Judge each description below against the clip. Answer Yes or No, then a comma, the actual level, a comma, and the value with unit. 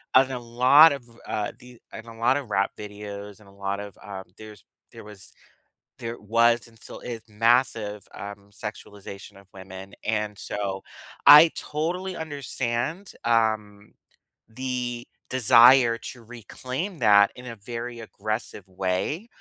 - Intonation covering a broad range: No, average, 3.4 semitones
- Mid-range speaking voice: No, low, 115 Hz